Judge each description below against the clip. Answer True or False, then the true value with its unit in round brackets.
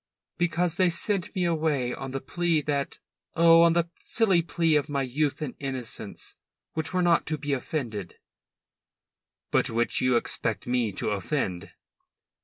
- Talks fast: False (155 wpm)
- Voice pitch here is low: False (150 Hz)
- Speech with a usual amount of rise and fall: True (4.8 semitones)